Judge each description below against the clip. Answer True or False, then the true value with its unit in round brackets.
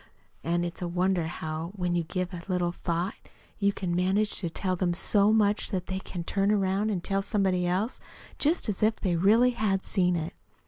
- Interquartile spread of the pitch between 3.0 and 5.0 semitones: False (2.5 semitones)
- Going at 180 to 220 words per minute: True (200 wpm)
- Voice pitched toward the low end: False (185 Hz)